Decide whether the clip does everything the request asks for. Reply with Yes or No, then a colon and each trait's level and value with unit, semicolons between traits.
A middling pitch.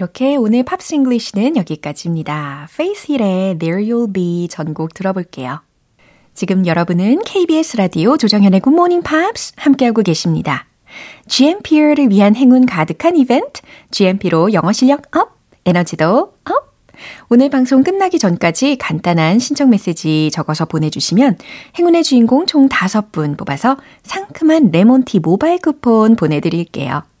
No: high, 220 Hz